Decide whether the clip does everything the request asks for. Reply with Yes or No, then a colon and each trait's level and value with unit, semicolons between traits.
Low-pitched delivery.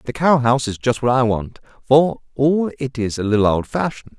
Yes: low, 125 Hz